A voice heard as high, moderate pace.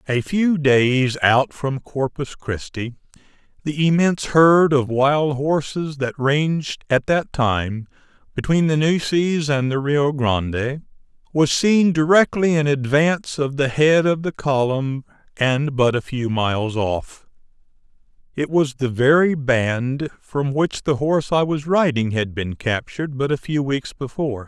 No: medium, 140 Hz; average, 150 wpm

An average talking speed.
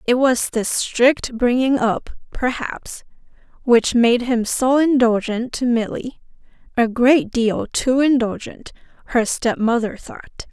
No: slow, 125 wpm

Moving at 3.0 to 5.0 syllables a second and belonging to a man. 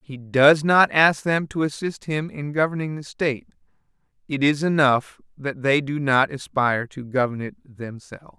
Yes: 4.7 syllables/s; male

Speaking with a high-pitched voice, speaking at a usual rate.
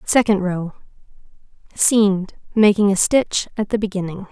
No: high, 200 Hz; slow, 110 wpm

